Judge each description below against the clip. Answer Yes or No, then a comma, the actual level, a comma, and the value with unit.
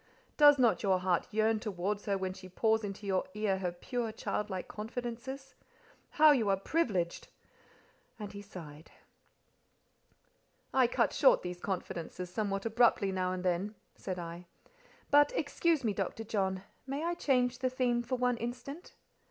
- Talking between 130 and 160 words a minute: Yes, average, 150 wpm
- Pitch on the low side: No, high, 210 Hz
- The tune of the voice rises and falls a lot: No, average, 4.8 semitones